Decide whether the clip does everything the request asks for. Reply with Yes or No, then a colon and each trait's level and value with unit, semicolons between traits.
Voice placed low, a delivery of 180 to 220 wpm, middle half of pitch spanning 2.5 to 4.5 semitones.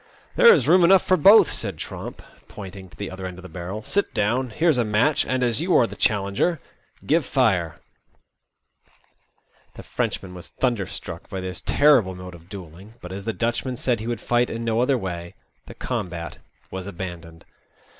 No: low, 105 Hz; average, 185 wpm; wide, 5.6 semitones